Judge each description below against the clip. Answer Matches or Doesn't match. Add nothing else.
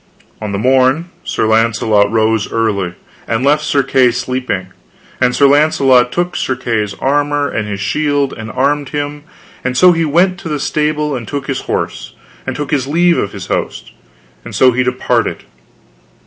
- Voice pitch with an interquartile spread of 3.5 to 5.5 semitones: Matches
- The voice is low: Matches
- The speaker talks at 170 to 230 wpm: Matches